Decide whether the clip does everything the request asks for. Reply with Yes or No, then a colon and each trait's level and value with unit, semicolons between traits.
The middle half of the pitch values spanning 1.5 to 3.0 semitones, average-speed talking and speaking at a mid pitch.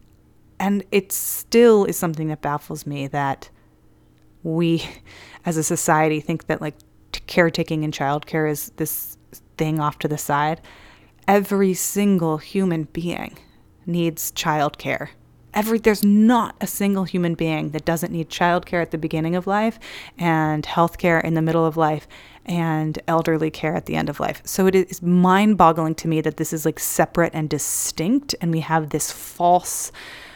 Yes: narrow, 2.6 semitones; average, 170 wpm; medium, 165 Hz